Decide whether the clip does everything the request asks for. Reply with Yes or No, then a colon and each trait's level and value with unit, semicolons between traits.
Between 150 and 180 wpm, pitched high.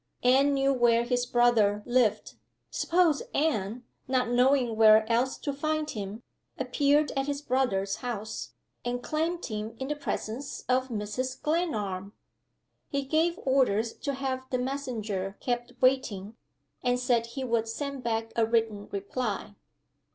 No: average, 140 wpm; high, 245 Hz